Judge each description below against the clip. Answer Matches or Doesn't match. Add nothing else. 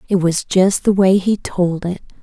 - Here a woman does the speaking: Matches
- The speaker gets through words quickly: Matches